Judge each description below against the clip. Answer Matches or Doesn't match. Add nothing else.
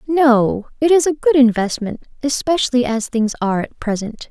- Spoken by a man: Doesn't match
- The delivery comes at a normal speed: Matches